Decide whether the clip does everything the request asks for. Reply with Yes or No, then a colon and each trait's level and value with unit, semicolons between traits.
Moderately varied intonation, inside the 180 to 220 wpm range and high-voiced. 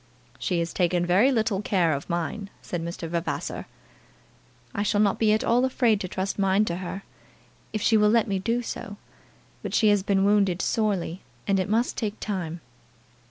Yes: average, 3.3 semitones; average, 185 wpm; high, 200 Hz